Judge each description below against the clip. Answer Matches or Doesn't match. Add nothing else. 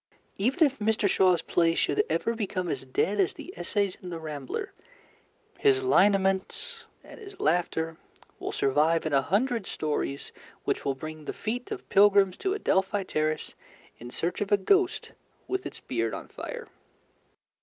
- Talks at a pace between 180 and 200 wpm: Doesn't match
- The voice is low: Doesn't match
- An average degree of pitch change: Doesn't match